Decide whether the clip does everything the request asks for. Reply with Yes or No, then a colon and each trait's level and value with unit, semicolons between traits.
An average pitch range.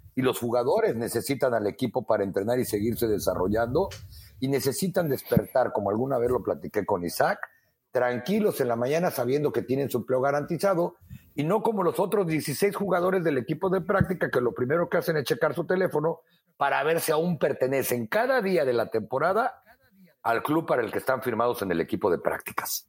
No: wide, 6.3 semitones